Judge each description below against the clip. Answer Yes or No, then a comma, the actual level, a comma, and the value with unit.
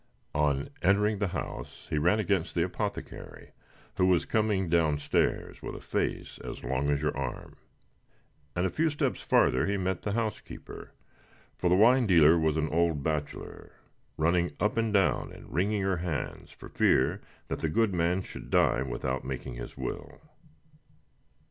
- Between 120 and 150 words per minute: No, average, 165 wpm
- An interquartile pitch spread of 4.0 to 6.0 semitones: Yes, average, 5.1 semitones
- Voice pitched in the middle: No, very low, 85 Hz